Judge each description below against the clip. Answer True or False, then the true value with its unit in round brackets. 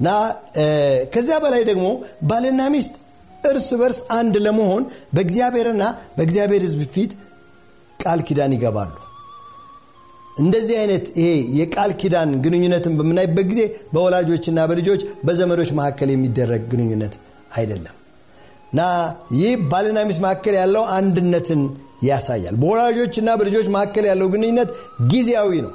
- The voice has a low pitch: False (185 Hz)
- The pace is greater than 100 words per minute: True (110 wpm)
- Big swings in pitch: True (7.2 semitones)